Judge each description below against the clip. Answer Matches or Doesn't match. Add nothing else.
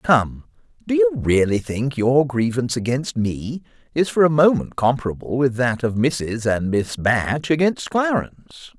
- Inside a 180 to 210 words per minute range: Doesn't match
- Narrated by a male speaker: Matches